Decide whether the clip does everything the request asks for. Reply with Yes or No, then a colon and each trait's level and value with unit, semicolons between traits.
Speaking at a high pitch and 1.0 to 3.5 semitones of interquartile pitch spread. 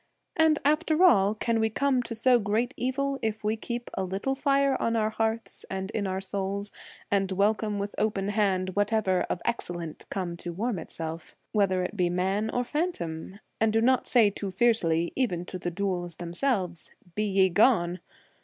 No: high, 205 Hz; average, 4.1 semitones